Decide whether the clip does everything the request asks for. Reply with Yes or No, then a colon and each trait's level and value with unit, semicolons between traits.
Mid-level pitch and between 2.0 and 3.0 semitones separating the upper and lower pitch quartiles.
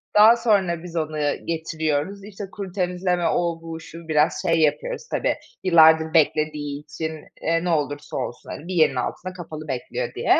Yes: medium, 165 Hz; average, 2.7 semitones